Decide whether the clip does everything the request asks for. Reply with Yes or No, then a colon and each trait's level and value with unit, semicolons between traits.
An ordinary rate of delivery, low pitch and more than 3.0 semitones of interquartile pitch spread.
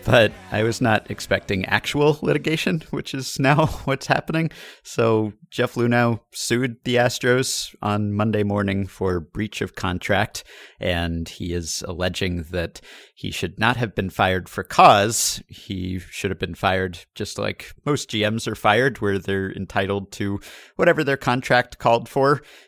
Yes: average, 155 wpm; low, 110 Hz; average, 5.2 semitones